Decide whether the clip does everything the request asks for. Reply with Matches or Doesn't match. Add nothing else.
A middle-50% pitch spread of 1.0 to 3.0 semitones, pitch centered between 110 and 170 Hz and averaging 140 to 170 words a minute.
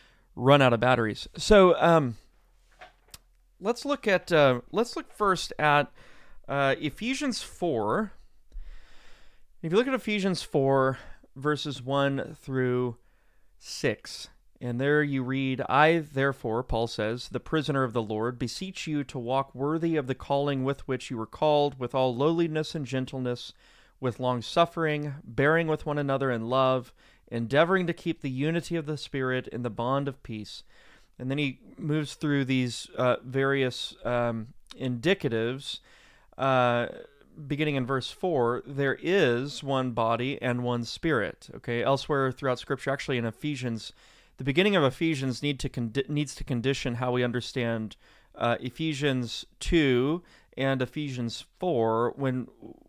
Doesn't match